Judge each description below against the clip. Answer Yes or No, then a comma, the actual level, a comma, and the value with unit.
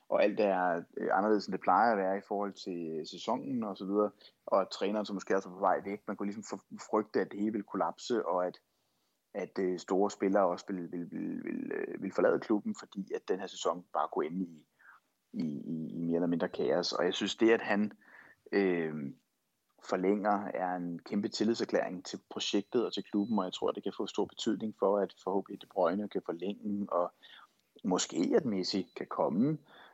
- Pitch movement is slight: Yes, narrow, 2.3 semitones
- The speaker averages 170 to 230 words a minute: Yes, average, 200 wpm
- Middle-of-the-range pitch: No, very low, 95 Hz